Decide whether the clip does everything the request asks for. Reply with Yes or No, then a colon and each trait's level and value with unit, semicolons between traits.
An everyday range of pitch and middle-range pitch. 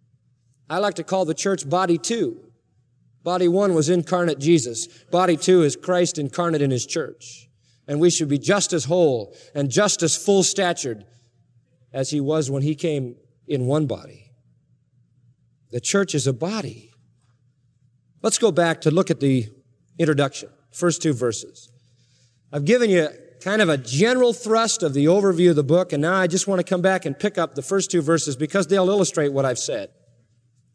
No: wide, 6.2 semitones; medium, 155 Hz